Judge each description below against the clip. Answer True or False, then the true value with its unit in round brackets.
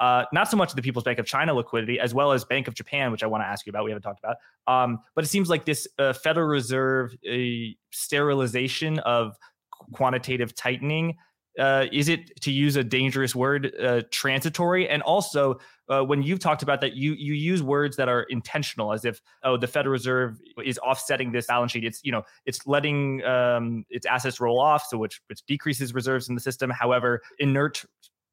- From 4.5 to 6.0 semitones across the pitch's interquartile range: False (2.9 semitones)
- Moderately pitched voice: False (130 Hz)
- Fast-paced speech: True (210 wpm)